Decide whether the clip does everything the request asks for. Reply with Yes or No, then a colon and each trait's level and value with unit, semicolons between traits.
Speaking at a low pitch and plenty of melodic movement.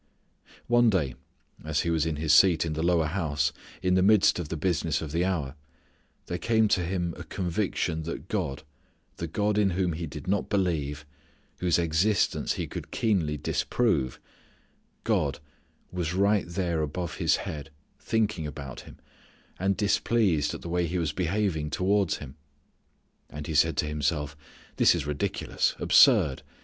No: very low, 85 Hz; average, 4.0 semitones